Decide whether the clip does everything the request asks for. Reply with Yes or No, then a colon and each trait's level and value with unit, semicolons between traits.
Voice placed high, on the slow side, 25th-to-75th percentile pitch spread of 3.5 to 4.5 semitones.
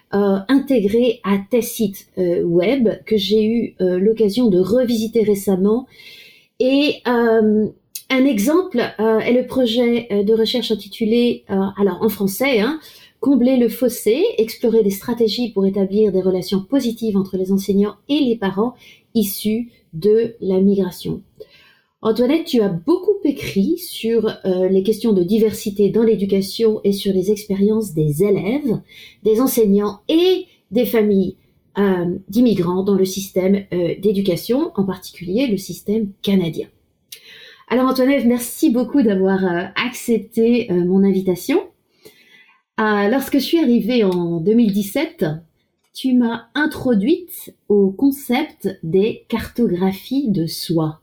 Yes: high, 220 Hz; slow, 135 wpm; average, 3.9 semitones